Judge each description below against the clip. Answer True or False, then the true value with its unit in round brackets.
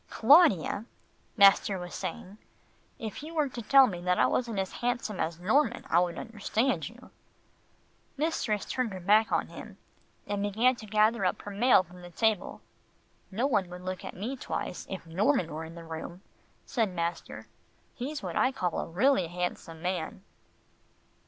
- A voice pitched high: True (200 Hz)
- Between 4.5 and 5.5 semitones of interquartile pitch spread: True (5.1 semitones)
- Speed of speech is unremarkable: True (170 wpm)